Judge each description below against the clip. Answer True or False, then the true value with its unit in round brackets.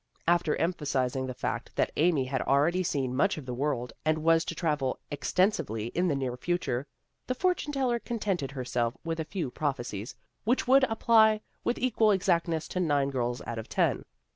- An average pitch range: False (6.1 semitones)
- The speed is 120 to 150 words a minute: False (190 wpm)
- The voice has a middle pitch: True (155 Hz)